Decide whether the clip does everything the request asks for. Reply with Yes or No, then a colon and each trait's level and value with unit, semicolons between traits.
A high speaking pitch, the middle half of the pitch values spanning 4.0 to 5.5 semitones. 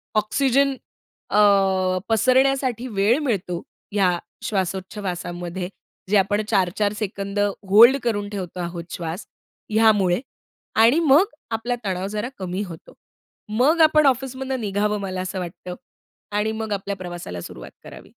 Yes: high, 205 Hz; average, 4.3 semitones